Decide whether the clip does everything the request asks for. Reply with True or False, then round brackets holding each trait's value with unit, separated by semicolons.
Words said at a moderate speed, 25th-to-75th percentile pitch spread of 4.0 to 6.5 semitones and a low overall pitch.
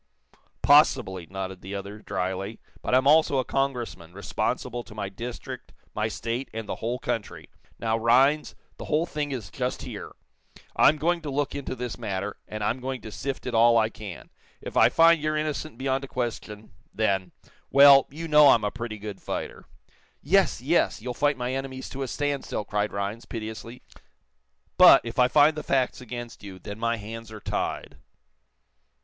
True (180 wpm; 4.4 semitones; 120 Hz)